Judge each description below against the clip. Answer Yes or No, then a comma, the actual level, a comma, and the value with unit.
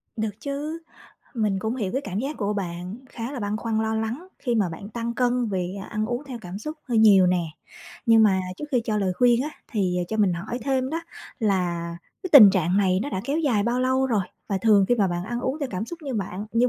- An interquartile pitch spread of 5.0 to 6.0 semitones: No, average, 4.4 semitones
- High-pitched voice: Yes, high, 220 Hz